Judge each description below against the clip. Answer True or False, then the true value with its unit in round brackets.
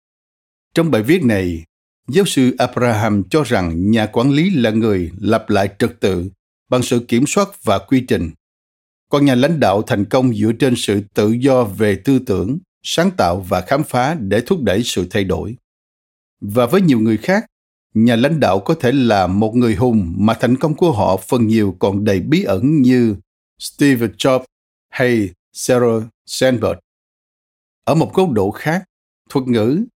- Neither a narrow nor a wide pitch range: True (4.9 semitones)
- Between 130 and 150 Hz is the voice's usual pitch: False (115 Hz)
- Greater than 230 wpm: False (175 wpm)